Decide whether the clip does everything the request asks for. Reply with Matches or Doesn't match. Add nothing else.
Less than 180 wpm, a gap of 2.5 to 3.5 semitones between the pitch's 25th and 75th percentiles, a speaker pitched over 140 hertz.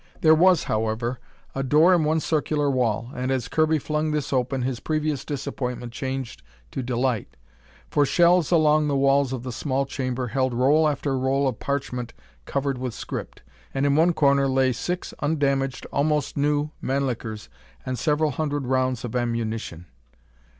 Doesn't match